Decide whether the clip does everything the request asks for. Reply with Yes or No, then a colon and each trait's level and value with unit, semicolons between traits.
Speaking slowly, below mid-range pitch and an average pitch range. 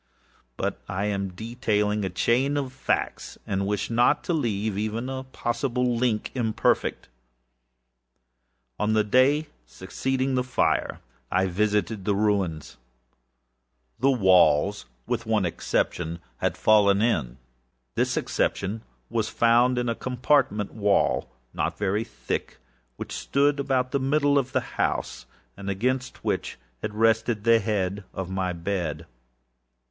Yes: slow, 130 wpm; low, 110 Hz; average, 4.4 semitones